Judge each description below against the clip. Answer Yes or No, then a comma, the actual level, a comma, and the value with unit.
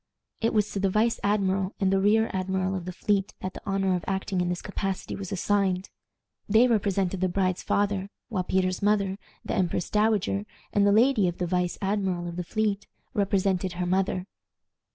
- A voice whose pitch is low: No, high, 195 Hz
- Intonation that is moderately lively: No, narrow, 1.8 semitones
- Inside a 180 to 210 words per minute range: Yes, average, 190 wpm